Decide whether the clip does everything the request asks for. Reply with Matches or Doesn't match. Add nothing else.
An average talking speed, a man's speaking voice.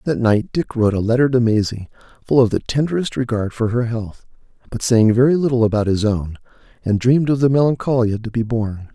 Doesn't match